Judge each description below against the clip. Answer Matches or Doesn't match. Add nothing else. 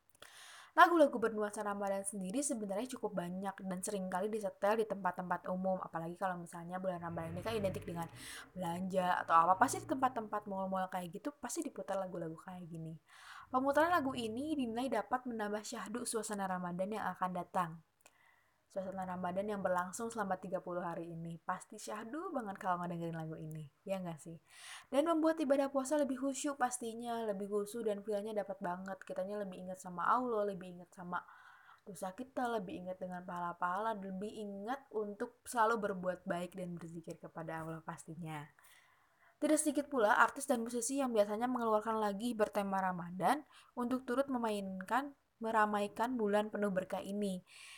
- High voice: Matches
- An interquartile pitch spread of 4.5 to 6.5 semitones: Matches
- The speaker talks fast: Matches